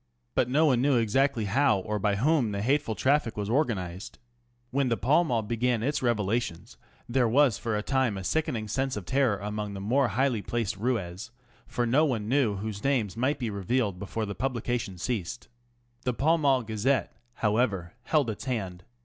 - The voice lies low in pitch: Yes, low, 115 Hz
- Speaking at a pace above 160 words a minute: Yes, average, 185 wpm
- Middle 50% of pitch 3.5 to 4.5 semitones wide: Yes, average, 4.2 semitones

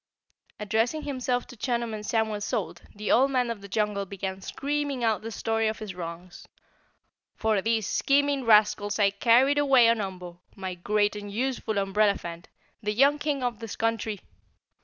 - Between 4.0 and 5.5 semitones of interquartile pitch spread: No, average, 3.5 semitones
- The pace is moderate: Yes, average, 165 wpm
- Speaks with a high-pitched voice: Yes, high, 220 Hz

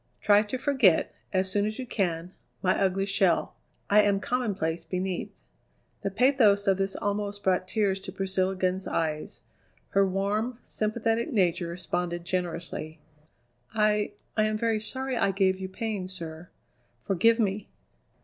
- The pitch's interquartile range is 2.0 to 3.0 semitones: Yes, narrow, 2.6 semitones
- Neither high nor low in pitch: No, high, 195 Hz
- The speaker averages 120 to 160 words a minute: Yes, average, 145 wpm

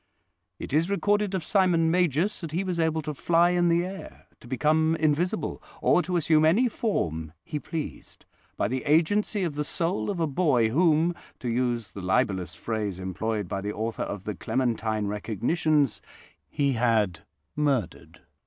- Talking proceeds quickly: No, average, 165 wpm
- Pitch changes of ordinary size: No, wide, 7.4 semitones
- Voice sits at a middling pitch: Yes, medium, 150 Hz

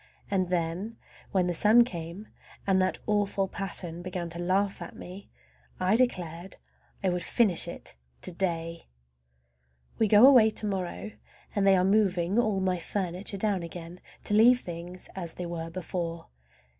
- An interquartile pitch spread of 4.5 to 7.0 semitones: No, average, 2.9 semitones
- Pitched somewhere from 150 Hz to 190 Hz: Yes, medium, 185 Hz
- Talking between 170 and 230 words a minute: No, average, 155 wpm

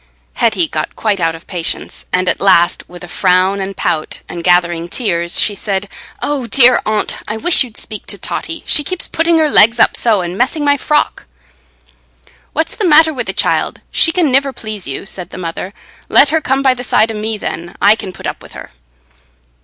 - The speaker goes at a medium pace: No, fast, 210 wpm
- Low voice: No, high, 215 Hz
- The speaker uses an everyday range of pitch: No, wide, 7.2 semitones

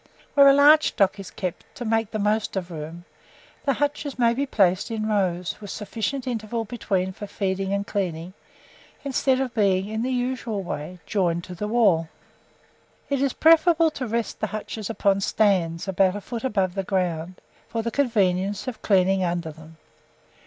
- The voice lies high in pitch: Yes, high, 205 Hz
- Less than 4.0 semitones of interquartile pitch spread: No, average, 4.5 semitones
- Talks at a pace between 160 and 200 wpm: Yes, average, 180 wpm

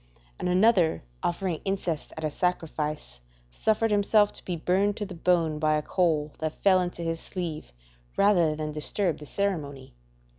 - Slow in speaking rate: No, average, 160 wpm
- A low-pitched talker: No, medium, 170 Hz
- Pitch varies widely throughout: No, average, 4.0 semitones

